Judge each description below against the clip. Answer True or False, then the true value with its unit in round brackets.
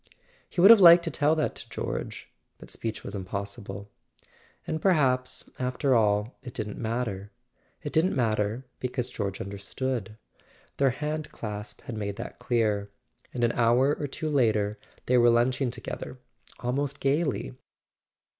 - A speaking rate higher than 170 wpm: False (145 wpm)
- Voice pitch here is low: True (120 Hz)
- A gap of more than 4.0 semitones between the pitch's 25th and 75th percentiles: True (4.8 semitones)